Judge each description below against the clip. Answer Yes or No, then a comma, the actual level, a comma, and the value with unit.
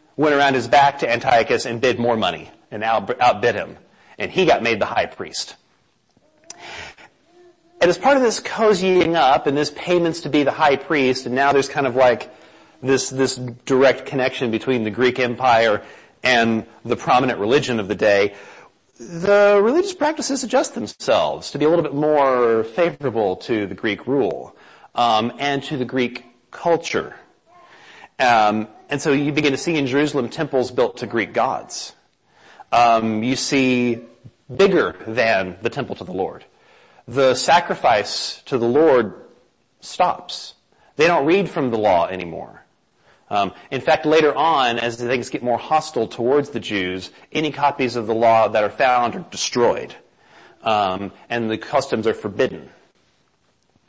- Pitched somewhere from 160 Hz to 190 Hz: No, low, 135 Hz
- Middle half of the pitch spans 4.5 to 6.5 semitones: Yes, average, 5.0 semitones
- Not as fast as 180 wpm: Yes, average, 160 wpm